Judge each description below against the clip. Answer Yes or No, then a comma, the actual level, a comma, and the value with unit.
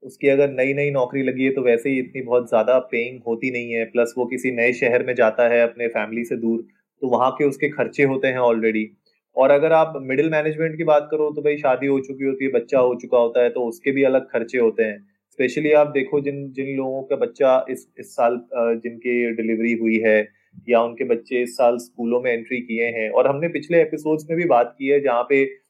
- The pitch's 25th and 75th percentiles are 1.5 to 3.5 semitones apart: Yes, average, 2.9 semitones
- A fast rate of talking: Yes, fast, 235 wpm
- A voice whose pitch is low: Yes, low, 130 Hz